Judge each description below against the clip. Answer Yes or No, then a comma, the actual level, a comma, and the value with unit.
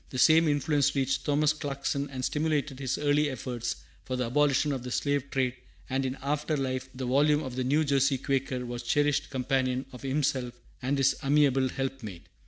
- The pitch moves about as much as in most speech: No, narrow, 2.2 semitones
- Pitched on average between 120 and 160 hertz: Yes, low, 135 Hz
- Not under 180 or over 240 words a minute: Yes, average, 190 wpm